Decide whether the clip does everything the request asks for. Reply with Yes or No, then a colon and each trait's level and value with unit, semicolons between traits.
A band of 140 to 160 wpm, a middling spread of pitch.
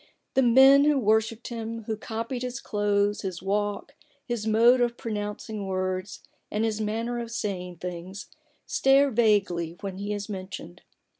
Yes: average, 155 wpm; average, 3.3 semitones